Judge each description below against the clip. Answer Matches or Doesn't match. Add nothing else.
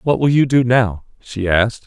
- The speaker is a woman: Doesn't match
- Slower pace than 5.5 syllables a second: Matches